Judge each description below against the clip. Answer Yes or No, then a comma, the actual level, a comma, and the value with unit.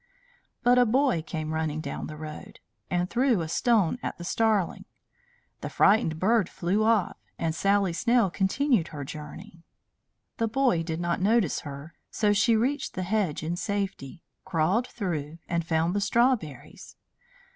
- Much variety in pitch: Yes, wide, 5.8 semitones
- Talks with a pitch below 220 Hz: Yes, medium, 185 Hz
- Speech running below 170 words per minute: Yes, average, 155 wpm